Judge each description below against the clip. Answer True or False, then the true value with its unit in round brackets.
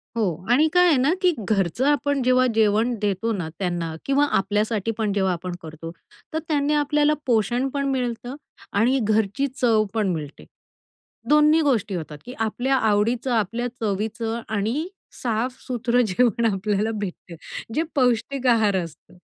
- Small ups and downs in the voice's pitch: False (4.4 semitones)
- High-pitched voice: True (230 Hz)